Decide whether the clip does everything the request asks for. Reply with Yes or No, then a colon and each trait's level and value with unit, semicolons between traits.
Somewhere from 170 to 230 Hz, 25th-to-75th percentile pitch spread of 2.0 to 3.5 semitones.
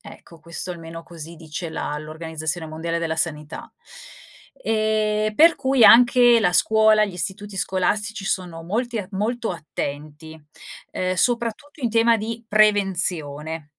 No: high, 190 Hz; average, 5.1 semitones